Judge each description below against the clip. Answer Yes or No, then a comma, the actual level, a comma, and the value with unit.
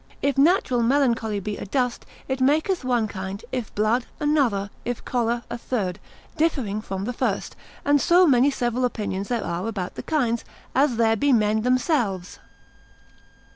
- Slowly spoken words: No, average, 155 wpm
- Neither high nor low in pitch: No, high, 240 Hz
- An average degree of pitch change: Yes, average, 4.3 semitones